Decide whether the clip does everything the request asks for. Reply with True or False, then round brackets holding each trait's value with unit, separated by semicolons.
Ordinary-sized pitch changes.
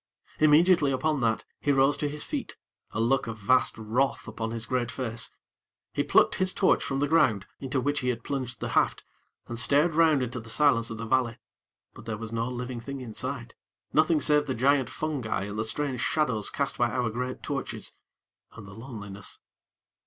True (3.9 semitones)